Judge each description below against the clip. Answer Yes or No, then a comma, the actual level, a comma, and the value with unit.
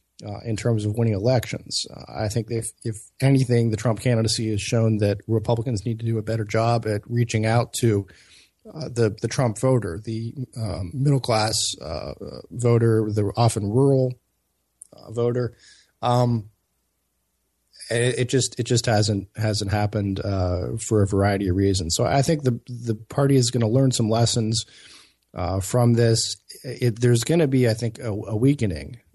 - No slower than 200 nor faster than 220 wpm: No, average, 175 wpm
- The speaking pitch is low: Yes, low, 115 Hz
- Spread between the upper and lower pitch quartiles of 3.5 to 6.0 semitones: No, average, 2.7 semitones